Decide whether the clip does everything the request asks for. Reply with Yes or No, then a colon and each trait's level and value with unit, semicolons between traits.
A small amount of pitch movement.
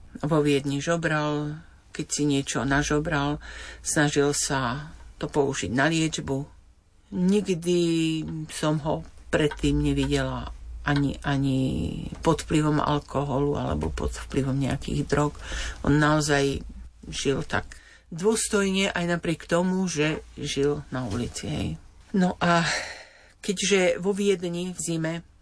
No: average, 3.5 semitones